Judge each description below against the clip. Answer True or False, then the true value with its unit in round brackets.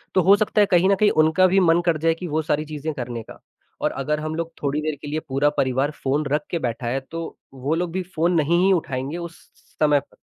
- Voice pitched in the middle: True (155 Hz)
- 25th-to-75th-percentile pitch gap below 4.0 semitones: True (3.1 semitones)